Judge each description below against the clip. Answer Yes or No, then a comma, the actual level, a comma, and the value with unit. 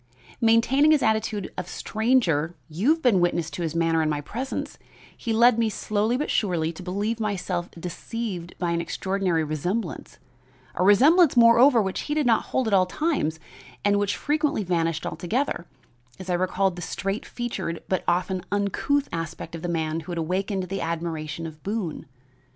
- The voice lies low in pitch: No, high, 190 Hz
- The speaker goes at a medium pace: Yes, average, 170 wpm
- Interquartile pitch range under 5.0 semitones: No, average, 5.3 semitones